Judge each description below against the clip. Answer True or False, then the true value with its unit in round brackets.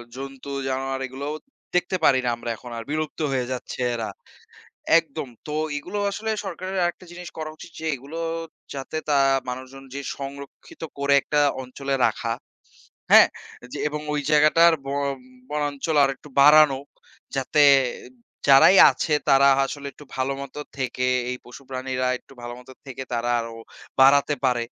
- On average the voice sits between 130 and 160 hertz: True (140 Hz)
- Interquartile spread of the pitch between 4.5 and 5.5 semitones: False (2.5 semitones)